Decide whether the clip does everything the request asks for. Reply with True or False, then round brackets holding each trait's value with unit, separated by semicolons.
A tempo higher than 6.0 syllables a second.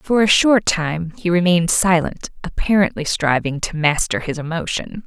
False (4.7 syllables/s)